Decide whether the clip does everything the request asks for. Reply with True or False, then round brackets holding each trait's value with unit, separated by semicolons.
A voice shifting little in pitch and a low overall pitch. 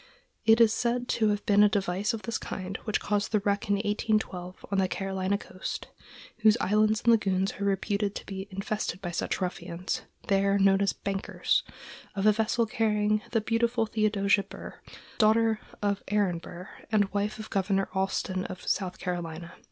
False (1.9 semitones; 200 Hz)